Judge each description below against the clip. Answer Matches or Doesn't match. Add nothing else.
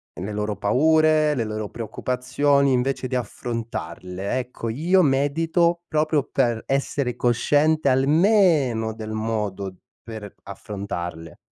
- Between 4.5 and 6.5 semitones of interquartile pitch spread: Matches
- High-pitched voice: Doesn't match